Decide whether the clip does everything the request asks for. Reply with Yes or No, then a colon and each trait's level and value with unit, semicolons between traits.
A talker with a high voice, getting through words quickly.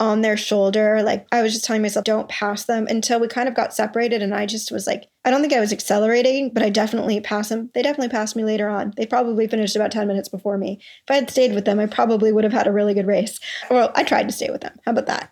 Yes: high, 215 Hz; fast, 285 wpm